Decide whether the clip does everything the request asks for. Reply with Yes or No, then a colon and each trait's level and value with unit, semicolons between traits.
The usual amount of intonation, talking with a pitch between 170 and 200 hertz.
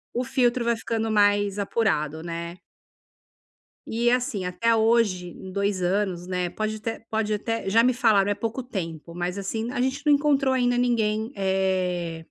No: average, 4.2 semitones; high, 210 Hz